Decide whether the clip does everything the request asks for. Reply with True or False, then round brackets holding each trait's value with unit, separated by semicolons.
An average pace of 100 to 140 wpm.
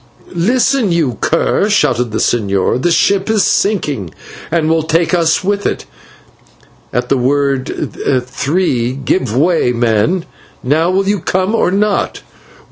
True (135 wpm)